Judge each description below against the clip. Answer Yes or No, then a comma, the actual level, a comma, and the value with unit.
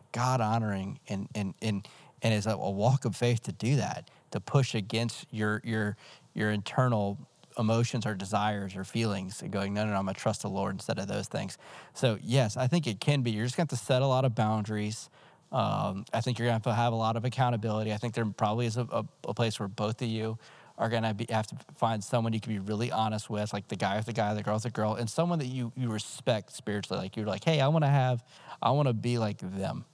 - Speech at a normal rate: No, fast, 255 wpm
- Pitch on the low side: Yes, low, 110 Hz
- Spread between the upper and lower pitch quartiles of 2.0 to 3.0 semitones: Yes, average, 2.7 semitones